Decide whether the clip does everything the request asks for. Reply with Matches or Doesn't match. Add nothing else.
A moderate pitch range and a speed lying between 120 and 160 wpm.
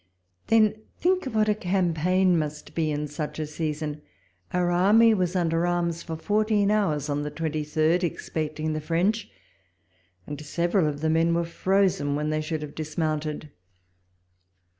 Matches